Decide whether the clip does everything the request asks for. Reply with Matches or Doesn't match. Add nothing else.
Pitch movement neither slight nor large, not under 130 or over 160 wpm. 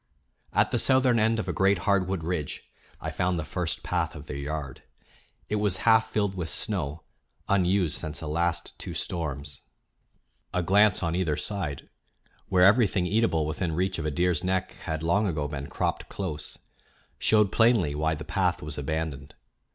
Doesn't match